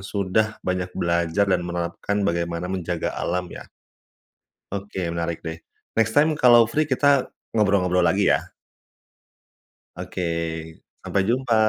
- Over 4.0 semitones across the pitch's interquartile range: Yes, average, 4.6 semitones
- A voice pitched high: No, very low, 95 Hz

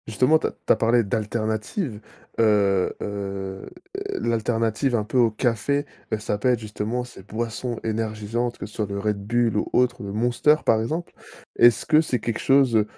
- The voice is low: Yes, low, 110 Hz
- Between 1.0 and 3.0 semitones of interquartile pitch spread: Yes, narrow, 2.5 semitones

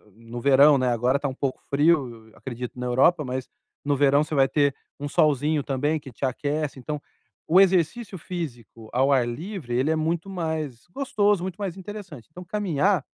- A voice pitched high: No, medium, 145 Hz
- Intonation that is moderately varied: Yes, average, 4.7 semitones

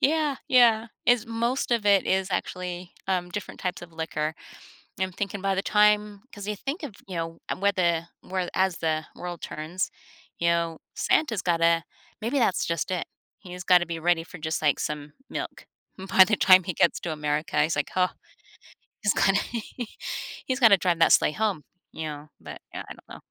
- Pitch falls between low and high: Yes, medium, 180 Hz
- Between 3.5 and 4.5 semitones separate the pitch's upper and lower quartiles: Yes, average, 3.8 semitones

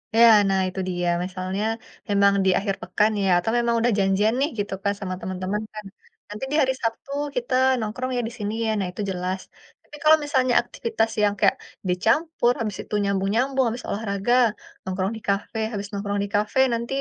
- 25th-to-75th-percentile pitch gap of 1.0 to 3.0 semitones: No, average, 3.5 semitones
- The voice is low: No, high, 210 Hz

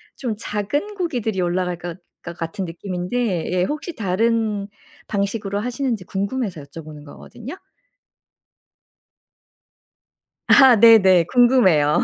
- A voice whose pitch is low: No, high, 200 Hz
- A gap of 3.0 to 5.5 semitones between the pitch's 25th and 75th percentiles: Yes, average, 5.2 semitones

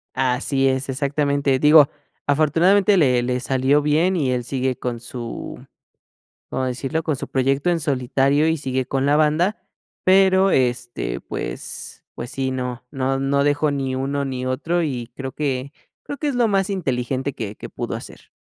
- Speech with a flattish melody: No, average, 3.0 semitones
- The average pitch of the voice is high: No, low, 135 Hz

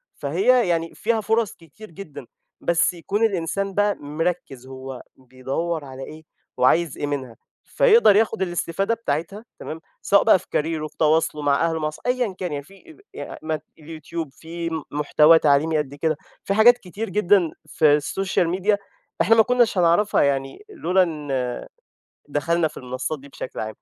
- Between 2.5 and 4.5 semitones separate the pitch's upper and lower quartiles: No, average, 5.3 semitones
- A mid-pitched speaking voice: Yes, medium, 165 Hz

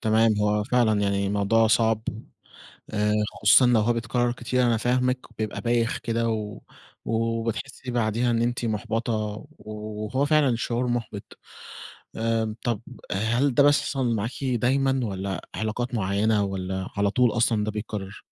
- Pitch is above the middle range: No, low, 115 Hz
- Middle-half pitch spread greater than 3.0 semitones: No, narrow, 2.4 semitones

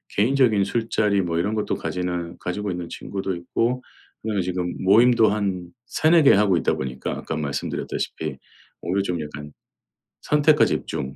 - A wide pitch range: No, average, 4.3 semitones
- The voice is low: Yes, very low, 95 Hz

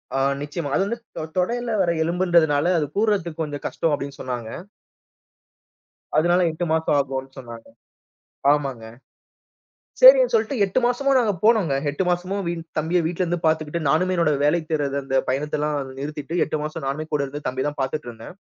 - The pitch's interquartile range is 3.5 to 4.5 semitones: Yes, average, 4.1 semitones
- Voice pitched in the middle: Yes, medium, 155 Hz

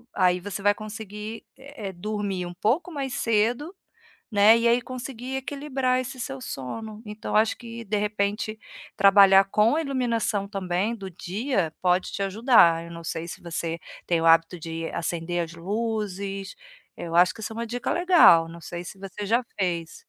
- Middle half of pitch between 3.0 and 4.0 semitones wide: No, average, 4.7 semitones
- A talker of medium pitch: No, high, 205 Hz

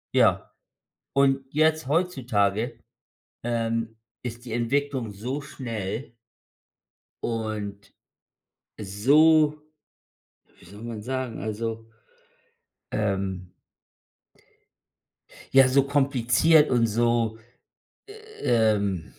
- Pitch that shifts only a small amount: No, average, 4.0 semitones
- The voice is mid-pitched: No, low, 115 Hz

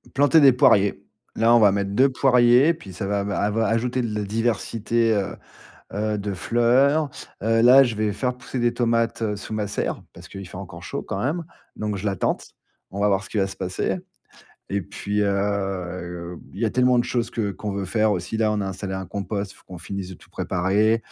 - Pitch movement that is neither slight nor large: Yes, average, 3.3 semitones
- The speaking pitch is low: Yes, low, 105 Hz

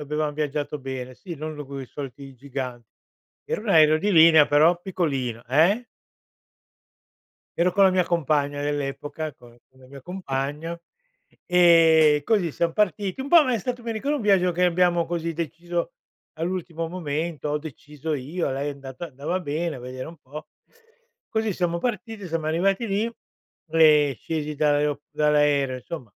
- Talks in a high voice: No, medium, 155 Hz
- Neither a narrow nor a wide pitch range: Yes, average, 3.7 semitones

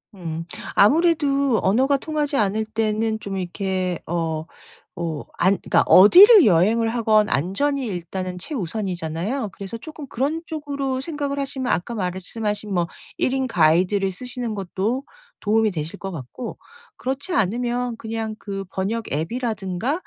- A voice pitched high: Yes, high, 215 Hz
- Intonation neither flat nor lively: No, wide, 5.9 semitones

